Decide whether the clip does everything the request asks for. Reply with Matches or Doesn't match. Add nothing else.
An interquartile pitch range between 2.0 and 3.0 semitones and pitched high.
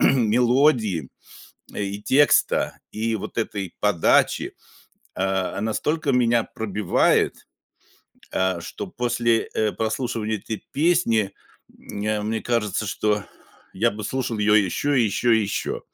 Doesn't match